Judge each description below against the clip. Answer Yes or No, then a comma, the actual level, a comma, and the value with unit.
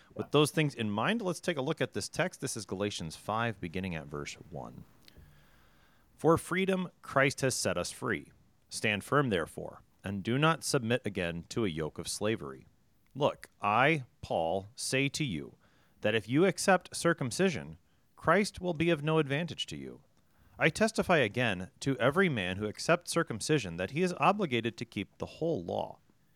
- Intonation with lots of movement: Yes, wide, 8.8 semitones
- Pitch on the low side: Yes, low, 125 Hz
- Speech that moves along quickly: No, average, 175 wpm